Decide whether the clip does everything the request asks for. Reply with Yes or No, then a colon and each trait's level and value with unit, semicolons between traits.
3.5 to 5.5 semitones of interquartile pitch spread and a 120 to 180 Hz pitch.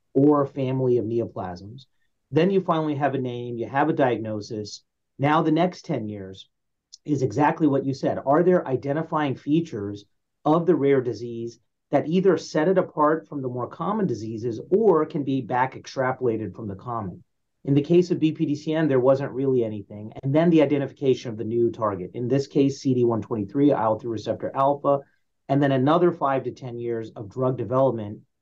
Yes: average, 4.2 semitones; low, 135 Hz